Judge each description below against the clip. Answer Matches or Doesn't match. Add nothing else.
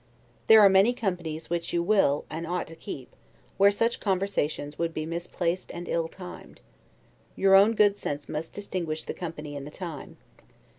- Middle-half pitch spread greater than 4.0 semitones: Doesn't match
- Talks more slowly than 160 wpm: Doesn't match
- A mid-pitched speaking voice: Matches